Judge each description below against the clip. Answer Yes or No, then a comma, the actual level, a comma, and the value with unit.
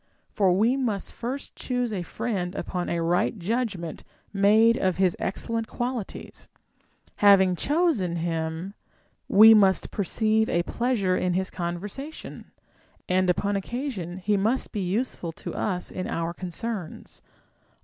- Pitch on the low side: No, high, 195 Hz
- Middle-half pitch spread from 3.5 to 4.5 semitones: Yes, average, 4.2 semitones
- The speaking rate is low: Yes, slow, 130 wpm